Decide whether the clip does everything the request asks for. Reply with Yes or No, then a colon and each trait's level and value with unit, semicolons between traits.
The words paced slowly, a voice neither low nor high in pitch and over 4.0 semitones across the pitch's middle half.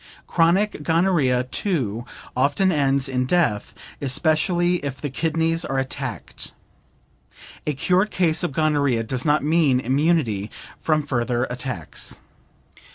Yes: slow, 115 wpm; medium, 145 Hz; average, 4.4 semitones